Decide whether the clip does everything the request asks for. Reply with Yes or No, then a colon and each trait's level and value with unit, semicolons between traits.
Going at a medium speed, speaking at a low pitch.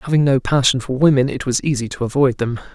No: fast, 240 wpm; low, 130 Hz